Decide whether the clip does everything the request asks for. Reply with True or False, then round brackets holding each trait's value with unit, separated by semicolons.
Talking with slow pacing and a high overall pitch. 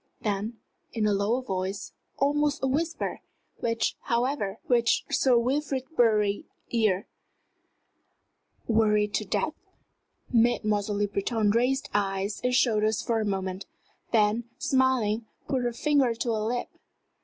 True (125 wpm; 230 Hz)